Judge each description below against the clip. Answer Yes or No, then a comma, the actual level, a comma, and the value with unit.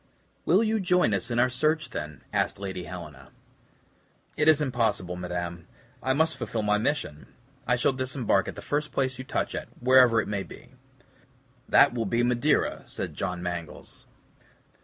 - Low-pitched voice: Yes, low, 120 Hz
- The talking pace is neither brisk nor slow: Yes, average, 165 wpm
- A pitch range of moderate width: No, wide, 7.3 semitones